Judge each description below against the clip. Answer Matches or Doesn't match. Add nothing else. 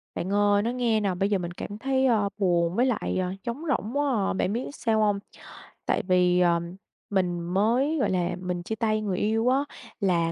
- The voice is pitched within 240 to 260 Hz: Doesn't match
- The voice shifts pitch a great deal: Doesn't match